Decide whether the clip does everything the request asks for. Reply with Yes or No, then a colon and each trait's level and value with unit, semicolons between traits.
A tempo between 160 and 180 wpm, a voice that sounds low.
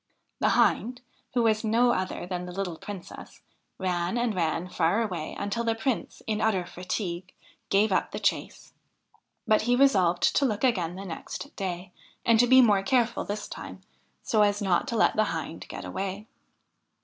No: average, 175 wpm; high, 205 Hz